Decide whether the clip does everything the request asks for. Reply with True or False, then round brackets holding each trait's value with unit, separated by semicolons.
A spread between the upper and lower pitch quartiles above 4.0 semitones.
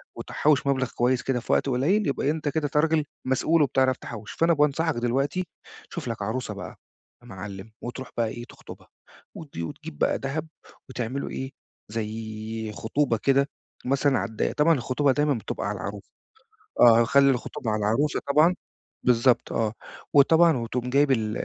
True (4.4 semitones)